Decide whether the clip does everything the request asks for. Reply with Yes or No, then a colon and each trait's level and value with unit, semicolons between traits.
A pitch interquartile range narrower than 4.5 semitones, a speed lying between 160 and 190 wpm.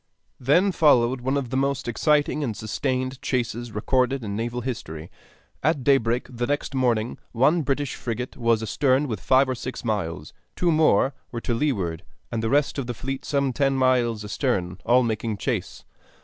Yes: average, 3.1 semitones; average, 175 wpm